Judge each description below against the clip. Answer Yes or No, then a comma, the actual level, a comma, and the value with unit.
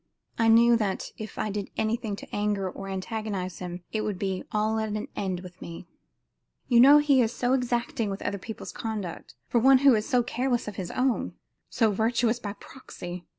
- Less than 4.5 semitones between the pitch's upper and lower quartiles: Yes, average, 3.5 semitones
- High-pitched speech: Yes, high, 215 Hz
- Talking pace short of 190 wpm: No, average, 200 wpm